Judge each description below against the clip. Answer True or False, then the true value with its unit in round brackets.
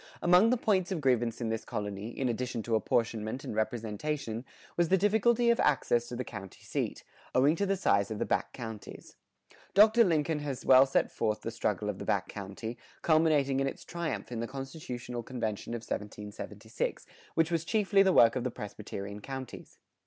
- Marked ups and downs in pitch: True (6.6 semitones)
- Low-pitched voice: True (125 Hz)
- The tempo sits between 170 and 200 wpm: True (185 wpm)